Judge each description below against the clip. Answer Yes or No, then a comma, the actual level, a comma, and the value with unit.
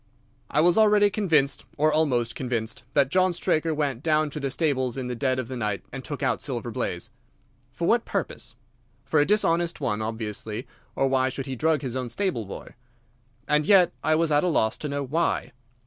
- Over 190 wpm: Yes, average, 200 wpm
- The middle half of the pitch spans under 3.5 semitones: No, average, 4.4 semitones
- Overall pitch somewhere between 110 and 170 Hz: Yes, medium, 140 Hz